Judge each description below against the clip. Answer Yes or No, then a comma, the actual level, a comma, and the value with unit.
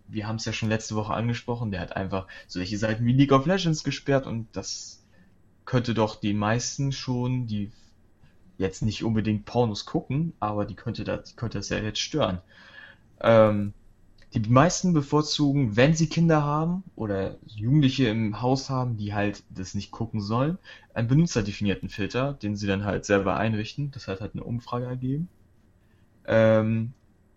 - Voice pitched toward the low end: Yes, low, 110 Hz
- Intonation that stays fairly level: No, average, 4.1 semitones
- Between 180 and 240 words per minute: No, average, 165 wpm